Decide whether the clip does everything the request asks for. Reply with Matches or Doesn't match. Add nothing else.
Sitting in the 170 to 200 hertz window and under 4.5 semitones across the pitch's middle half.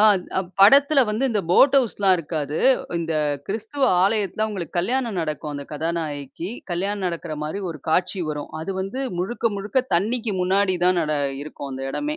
Doesn't match